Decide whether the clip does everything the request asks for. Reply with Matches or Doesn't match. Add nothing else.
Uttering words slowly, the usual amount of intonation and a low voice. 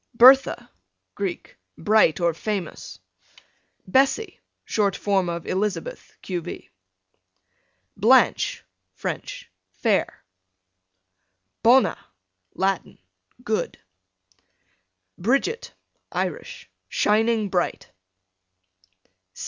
Doesn't match